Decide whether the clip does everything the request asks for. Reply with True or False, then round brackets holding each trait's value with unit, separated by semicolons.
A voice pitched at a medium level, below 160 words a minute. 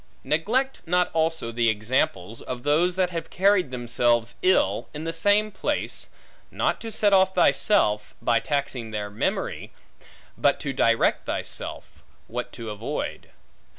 True (150 Hz; 140 wpm)